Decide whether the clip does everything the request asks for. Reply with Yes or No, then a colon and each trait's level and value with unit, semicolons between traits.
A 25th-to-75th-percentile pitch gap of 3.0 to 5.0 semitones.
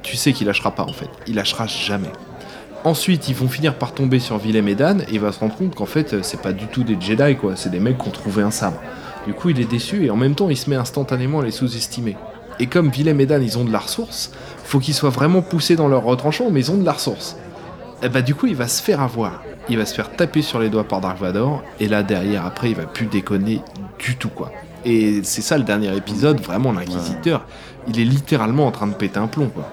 No: wide, 5.6 semitones